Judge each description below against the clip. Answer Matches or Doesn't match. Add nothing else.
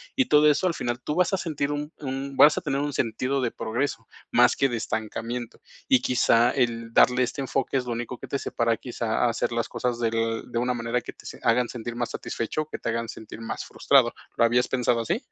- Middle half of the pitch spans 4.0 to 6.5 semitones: Doesn't match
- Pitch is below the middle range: Matches